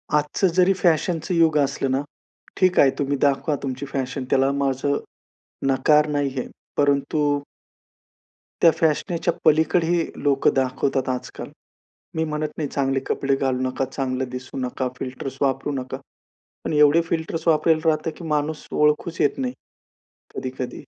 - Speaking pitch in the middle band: Yes, medium, 145 Hz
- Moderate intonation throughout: Yes, average, 3.0 semitones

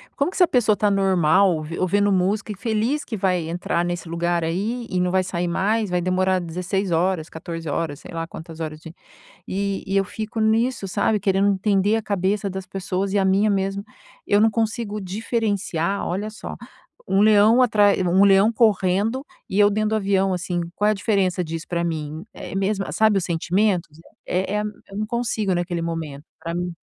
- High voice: Yes, high, 195 Hz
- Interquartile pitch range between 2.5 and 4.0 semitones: Yes, average, 3.1 semitones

